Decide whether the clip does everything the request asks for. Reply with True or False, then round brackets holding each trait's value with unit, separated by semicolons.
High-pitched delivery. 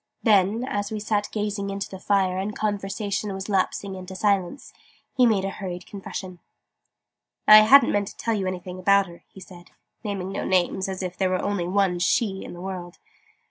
True (195 Hz)